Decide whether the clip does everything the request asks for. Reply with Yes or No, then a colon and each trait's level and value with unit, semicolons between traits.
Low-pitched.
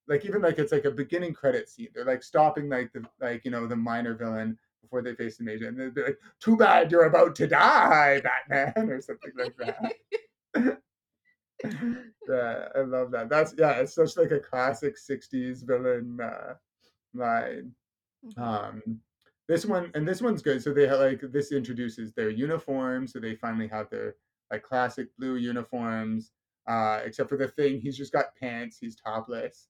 Yes: low, 130 Hz